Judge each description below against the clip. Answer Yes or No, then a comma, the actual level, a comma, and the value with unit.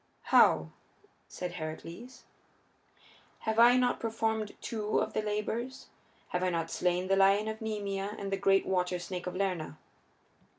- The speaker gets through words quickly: No, average, 145 wpm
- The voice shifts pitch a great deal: No, average, 3.4 semitones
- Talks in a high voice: Yes, high, 195 Hz